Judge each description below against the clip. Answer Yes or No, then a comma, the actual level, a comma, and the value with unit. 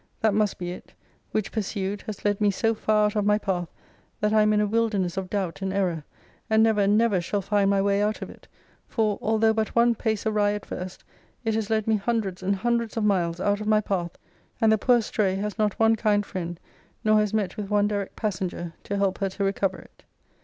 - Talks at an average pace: No, fast, 230 wpm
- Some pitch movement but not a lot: No, narrow, 1.9 semitones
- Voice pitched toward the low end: No, high, 205 Hz